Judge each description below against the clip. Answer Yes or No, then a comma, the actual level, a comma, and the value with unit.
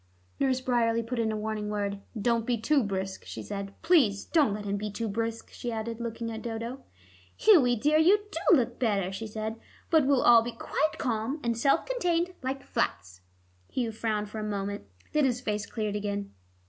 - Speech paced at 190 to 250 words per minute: Yes, average, 195 wpm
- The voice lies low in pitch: No, high, 230 Hz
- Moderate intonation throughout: Yes, average, 3.8 semitones